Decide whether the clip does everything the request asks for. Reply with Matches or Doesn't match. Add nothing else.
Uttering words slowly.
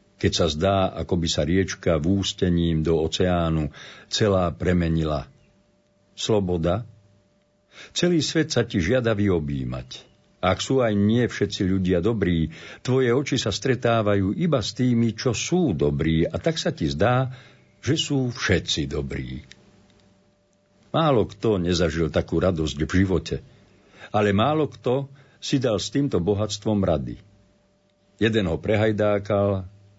Doesn't match